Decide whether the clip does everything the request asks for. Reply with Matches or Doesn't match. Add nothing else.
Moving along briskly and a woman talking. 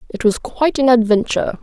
Doesn't match